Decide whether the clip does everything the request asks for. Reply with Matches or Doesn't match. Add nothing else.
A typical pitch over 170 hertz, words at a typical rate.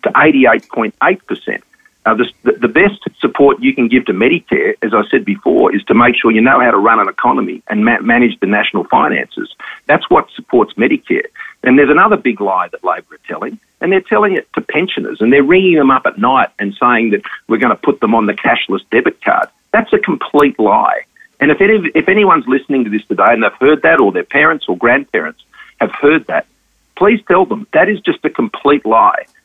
Doesn't match